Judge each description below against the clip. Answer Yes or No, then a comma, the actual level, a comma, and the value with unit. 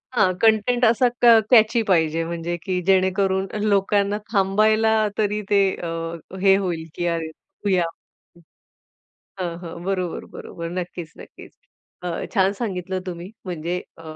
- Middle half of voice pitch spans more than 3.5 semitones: No, average, 3.1 semitones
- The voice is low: No, high, 190 Hz